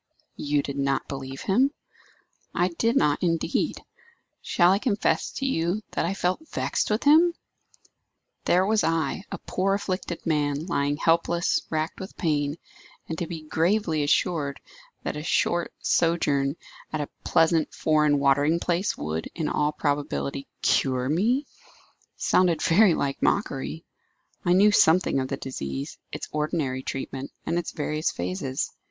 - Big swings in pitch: No, average, 4.3 semitones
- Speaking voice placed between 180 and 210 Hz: No, medium, 160 Hz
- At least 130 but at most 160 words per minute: Yes, average, 145 wpm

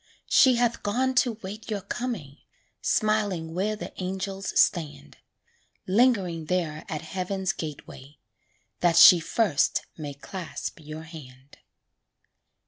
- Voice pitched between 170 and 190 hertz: Yes, medium, 185 Hz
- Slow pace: Yes, slow, 115 wpm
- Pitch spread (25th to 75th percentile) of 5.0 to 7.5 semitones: Yes, average, 5.3 semitones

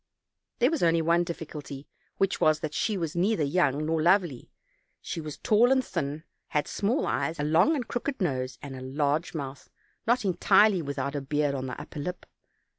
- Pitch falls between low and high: Yes, medium, 160 Hz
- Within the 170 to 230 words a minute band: Yes, average, 190 wpm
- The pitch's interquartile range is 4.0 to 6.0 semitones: Yes, average, 5.2 semitones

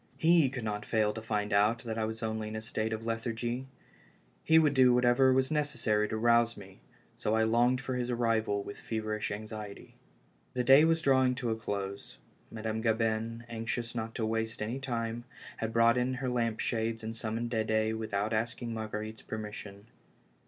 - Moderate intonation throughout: No, narrow, 1.8 semitones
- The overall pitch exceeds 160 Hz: No, low, 115 Hz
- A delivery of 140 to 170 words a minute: No, average, 185 wpm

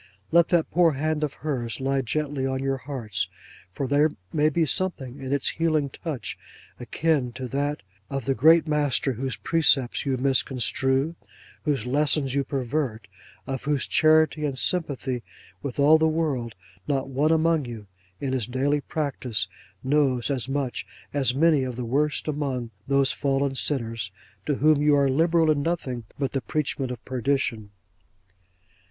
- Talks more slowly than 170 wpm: Yes, average, 160 wpm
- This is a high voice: No, medium, 140 Hz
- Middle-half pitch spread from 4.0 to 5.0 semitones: No, average, 2.7 semitones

